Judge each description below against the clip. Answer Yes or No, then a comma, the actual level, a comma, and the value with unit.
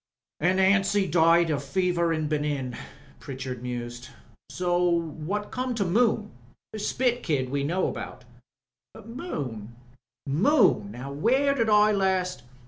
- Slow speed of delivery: Yes, slow, 125 wpm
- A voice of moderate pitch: Yes, medium, 170 Hz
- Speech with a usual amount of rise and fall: No, wide, 6.9 semitones